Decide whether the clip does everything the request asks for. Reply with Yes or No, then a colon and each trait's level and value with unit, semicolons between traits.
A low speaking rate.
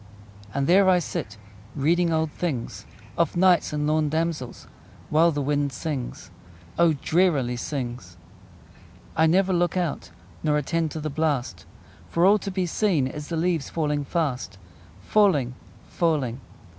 No: average, 145 wpm